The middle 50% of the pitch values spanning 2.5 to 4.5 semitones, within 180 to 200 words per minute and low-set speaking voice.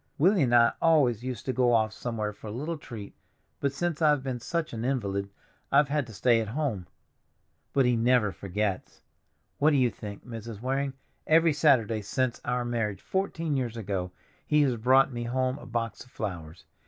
Yes: average, 4.1 semitones; average, 190 wpm; low, 120 Hz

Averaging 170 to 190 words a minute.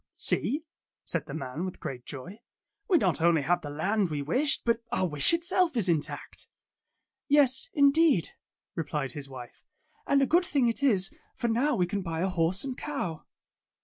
Yes: average, 180 wpm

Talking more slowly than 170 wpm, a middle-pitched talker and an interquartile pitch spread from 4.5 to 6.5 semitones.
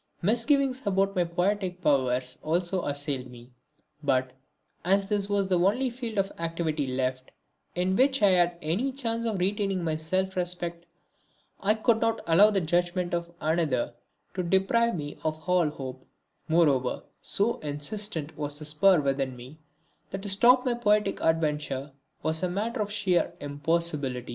Yes: average, 155 wpm; medium, 175 Hz; average, 5.3 semitones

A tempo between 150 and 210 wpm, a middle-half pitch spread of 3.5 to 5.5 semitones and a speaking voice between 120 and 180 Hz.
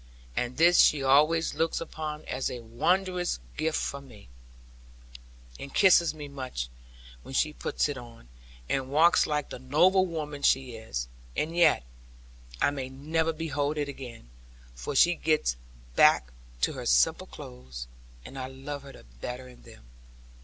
Yes: average, 155 wpm; average, 4.2 semitones; medium, 140 Hz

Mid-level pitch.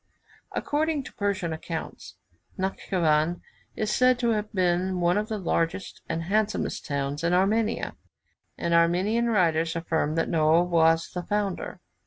Yes: medium, 180 Hz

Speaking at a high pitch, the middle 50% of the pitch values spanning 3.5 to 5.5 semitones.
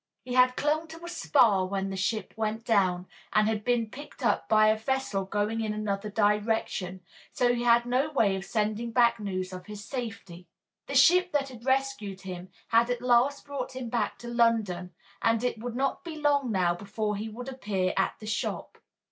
Yes: high, 225 Hz; average, 3.8 semitones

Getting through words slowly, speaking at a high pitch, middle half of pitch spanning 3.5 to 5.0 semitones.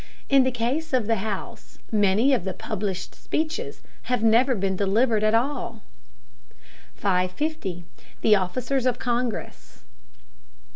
Yes: slow, 125 wpm; high, 225 Hz; average, 4.7 semitones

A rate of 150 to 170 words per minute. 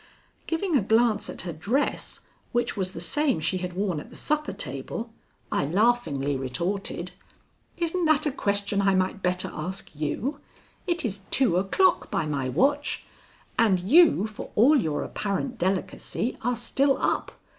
Yes: average, 155 wpm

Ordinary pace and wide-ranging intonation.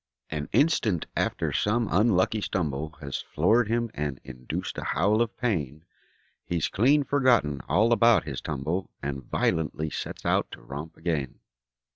Yes: average, 145 wpm; wide, 7.6 semitones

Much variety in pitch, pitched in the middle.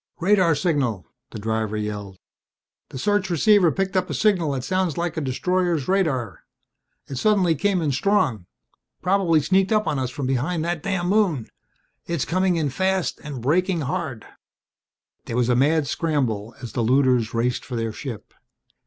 Yes: wide, 6.8 semitones; medium, 155 Hz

